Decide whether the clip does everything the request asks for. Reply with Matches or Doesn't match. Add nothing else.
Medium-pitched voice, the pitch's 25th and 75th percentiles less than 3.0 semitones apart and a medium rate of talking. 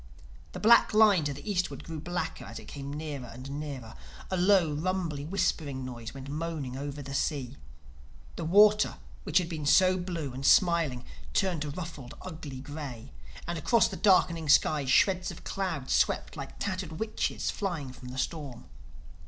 Doesn't match